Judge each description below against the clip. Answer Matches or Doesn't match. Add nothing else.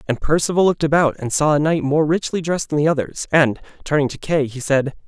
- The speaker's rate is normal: Doesn't match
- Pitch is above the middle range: Doesn't match